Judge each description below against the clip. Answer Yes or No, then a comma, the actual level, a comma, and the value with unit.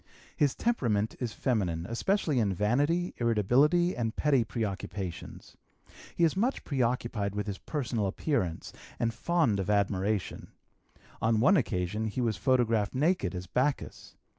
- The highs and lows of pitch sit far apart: Yes, wide, 5.8 semitones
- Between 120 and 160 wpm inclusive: Yes, slow, 135 wpm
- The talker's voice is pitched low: Yes, low, 115 Hz